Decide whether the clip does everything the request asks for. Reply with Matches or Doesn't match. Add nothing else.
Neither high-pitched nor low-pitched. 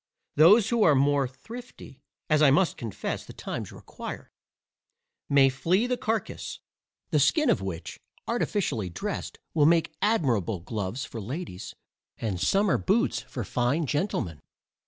Matches